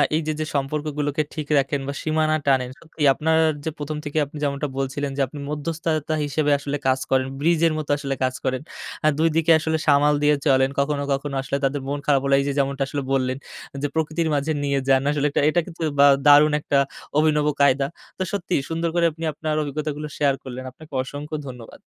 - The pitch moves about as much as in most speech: No, narrow, 2.1 semitones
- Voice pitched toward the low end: No, medium, 145 Hz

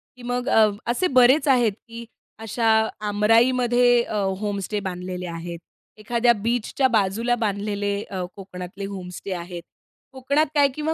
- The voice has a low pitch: No, high, 220 Hz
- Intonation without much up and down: No, average, 3.9 semitones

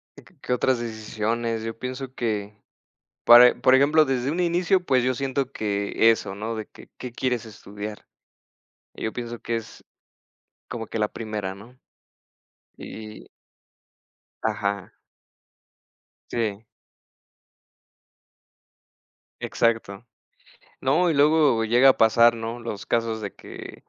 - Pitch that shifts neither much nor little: Yes, average, 3.0 semitones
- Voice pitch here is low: Yes, low, 115 Hz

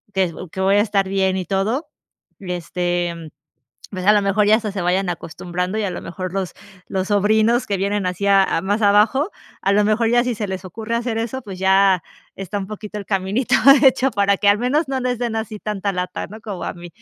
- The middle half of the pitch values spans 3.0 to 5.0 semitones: No, narrow, 2.6 semitones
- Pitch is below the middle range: No, high, 200 Hz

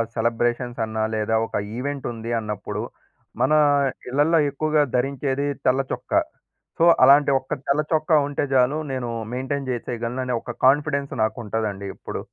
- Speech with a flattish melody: No, average, 3.4 semitones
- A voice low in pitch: Yes, low, 130 Hz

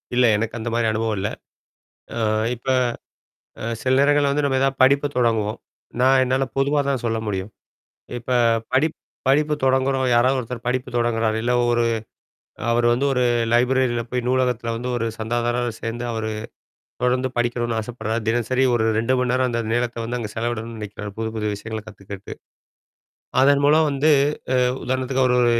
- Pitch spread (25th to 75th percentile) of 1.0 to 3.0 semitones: Yes, narrow, 2.5 semitones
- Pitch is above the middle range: No, low, 120 Hz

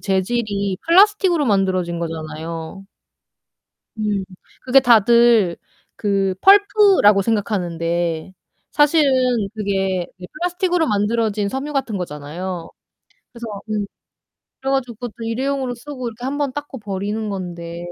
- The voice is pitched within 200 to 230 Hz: Yes, high, 215 Hz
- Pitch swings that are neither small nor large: No, wide, 6.1 semitones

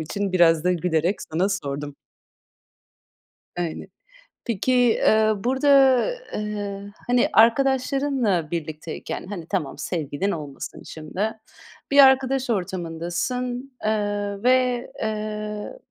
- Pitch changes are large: Yes, wide, 6.3 semitones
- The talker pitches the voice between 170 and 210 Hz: Yes, high, 205 Hz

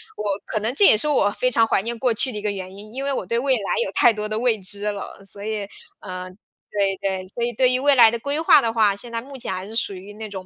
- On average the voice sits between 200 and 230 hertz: Yes, high, 215 Hz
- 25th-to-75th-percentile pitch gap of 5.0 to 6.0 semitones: No, average, 3.3 semitones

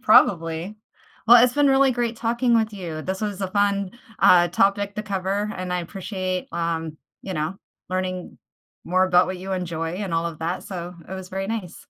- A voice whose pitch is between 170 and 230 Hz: Yes, medium, 185 Hz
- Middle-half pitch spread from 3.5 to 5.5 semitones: No, average, 2.8 semitones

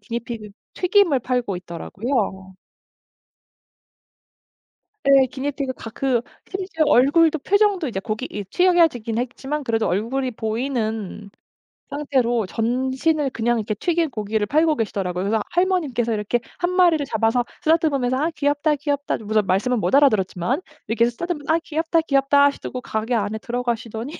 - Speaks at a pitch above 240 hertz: Yes, very high, 255 Hz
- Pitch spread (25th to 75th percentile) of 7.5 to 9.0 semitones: No, average, 5.2 semitones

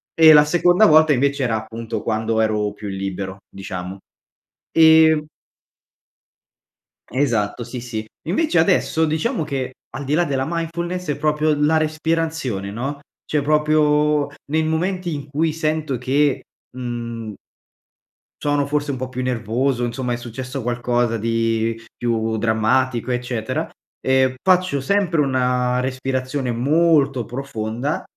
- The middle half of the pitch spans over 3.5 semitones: Yes, average, 4.7 semitones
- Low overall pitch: Yes, low, 130 Hz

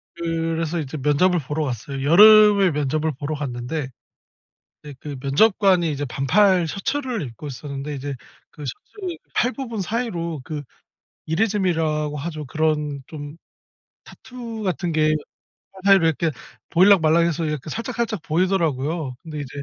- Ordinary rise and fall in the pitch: Yes, average, 4.7 semitones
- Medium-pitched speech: Yes, medium, 160 Hz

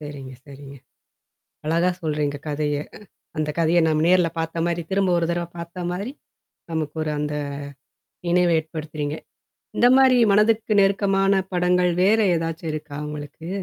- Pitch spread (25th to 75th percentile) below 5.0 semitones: Yes, average, 3.3 semitones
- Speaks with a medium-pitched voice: Yes, medium, 165 Hz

